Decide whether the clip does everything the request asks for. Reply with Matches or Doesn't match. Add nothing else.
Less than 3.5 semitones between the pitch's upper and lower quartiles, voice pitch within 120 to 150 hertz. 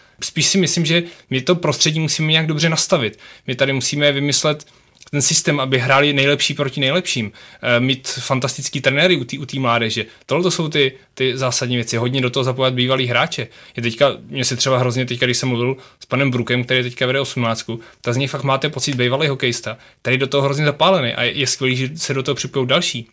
Matches